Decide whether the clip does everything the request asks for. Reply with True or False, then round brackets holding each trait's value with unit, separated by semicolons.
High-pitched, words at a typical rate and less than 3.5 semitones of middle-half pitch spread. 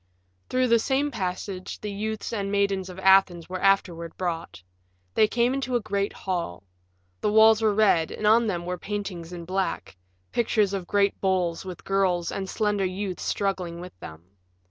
True (195 Hz; 170 wpm; 2.9 semitones)